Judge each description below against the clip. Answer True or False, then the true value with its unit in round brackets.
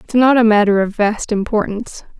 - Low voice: False (215 Hz)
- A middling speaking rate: True (190 wpm)